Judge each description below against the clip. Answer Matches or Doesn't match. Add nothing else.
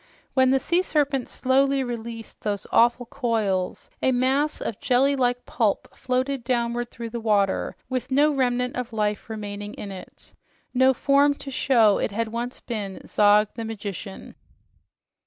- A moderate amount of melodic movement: Matches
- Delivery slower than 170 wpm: Matches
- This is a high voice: Matches